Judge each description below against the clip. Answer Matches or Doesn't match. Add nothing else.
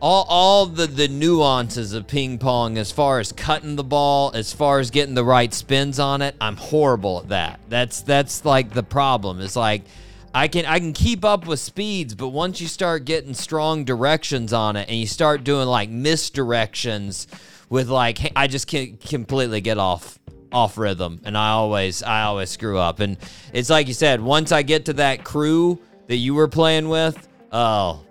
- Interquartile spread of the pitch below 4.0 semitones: Doesn't match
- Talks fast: Doesn't match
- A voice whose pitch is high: Doesn't match